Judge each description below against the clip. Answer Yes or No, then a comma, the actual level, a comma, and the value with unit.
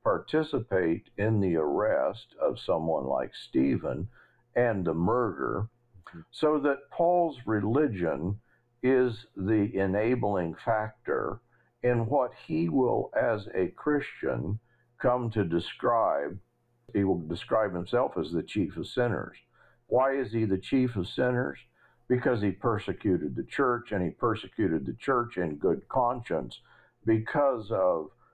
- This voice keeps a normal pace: No, slow, 125 wpm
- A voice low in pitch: Yes, low, 115 Hz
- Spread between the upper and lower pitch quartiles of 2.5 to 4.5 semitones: No, average, 5.0 semitones